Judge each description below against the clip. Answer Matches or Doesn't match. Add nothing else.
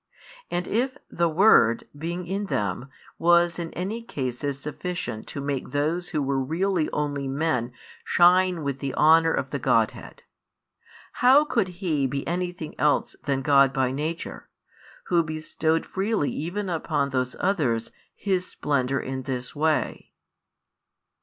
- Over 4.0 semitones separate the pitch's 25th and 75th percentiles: Matches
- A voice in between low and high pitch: Matches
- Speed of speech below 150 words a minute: Matches